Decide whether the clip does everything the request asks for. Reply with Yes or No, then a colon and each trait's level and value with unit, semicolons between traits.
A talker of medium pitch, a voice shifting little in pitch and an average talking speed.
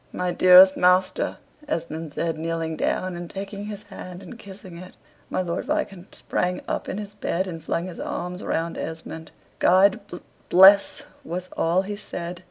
Yes: medium, 180 Hz; narrow, 2.3 semitones; average, 175 wpm